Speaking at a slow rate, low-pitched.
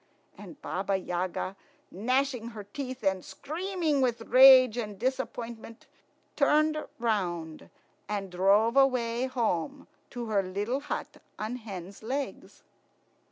No: slow, 115 wpm; high, 230 Hz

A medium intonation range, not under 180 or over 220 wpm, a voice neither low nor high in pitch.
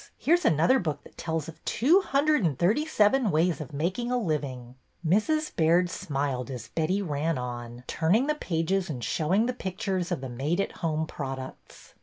No: wide, 6.5 semitones; average, 185 wpm; medium, 165 Hz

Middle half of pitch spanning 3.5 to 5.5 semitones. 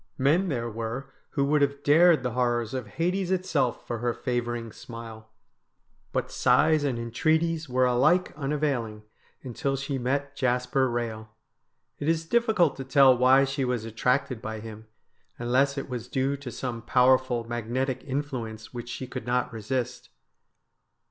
No: average, 3.0 semitones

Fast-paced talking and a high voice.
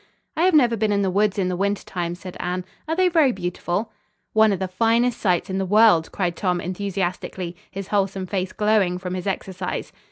Yes: fast, 210 wpm; high, 195 Hz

